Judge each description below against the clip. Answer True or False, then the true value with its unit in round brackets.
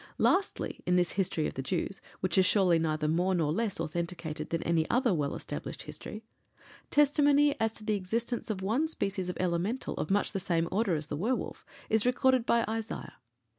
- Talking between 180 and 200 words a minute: True (190 wpm)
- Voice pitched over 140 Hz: True (190 Hz)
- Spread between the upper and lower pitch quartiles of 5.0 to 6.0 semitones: True (5.3 semitones)